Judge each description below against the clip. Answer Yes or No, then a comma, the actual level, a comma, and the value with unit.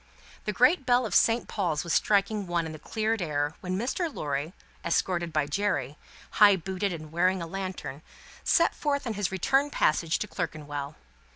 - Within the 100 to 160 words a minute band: No, average, 175 wpm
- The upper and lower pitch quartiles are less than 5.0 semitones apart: No, average, 5.3 semitones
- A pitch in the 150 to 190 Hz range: Yes, medium, 185 Hz